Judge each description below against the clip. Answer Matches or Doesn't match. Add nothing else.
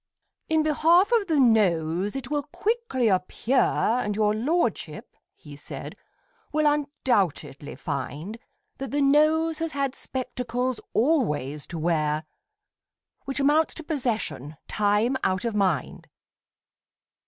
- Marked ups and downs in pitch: Matches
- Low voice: Doesn't match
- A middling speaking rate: Doesn't match